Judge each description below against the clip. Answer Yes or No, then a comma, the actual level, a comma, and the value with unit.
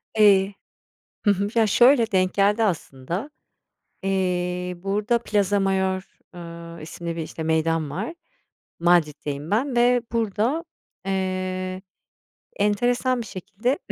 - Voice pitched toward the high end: Yes, high, 195 Hz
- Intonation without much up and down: No, average, 3.6 semitones